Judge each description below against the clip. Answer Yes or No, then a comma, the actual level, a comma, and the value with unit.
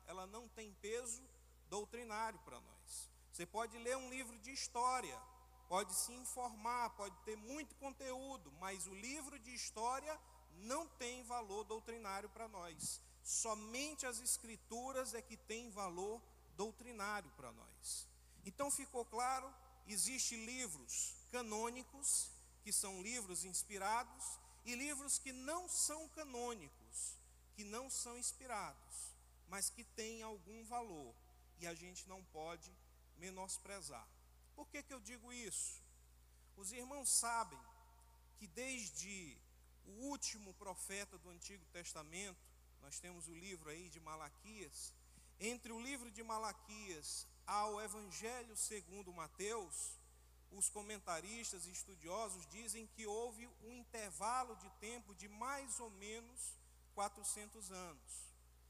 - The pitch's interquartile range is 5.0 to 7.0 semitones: Yes, wide, 5.5 semitones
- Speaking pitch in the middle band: No, high, 215 Hz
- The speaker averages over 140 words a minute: No, average, 125 wpm